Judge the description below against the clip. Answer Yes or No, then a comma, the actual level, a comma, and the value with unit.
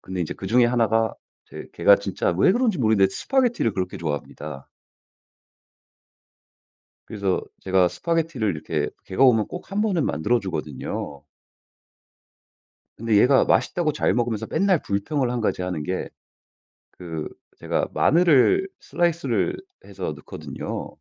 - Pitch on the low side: Yes, low, 110 Hz